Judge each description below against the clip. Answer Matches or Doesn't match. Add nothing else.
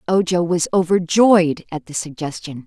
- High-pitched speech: Doesn't match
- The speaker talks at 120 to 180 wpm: Matches